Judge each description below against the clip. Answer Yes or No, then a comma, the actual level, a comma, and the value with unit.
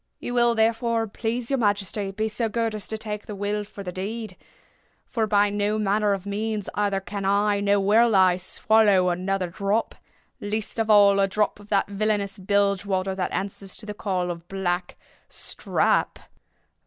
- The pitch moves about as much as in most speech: No, narrow, 1.8 semitones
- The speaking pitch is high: Yes, high, 205 Hz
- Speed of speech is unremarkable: Yes, average, 170 wpm